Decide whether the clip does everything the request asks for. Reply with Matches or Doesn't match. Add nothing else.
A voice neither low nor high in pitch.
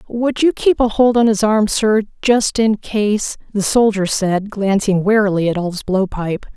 Doesn't match